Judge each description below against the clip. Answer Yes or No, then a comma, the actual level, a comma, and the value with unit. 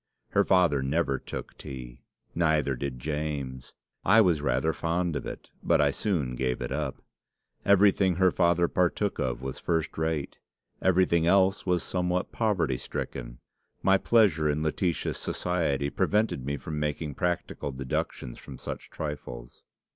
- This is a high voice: No, very low, 80 Hz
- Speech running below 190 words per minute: Yes, average, 145 wpm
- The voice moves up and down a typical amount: Yes, average, 4.9 semitones